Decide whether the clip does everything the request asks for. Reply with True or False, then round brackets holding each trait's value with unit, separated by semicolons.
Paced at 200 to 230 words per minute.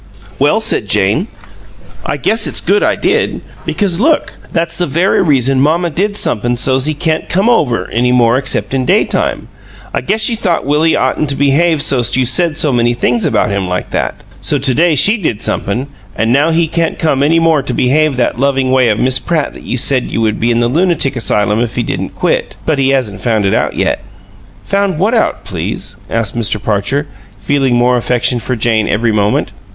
True (205 wpm)